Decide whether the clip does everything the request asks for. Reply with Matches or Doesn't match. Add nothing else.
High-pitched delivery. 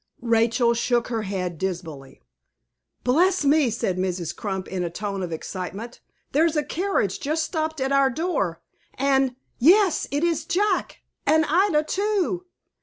Matches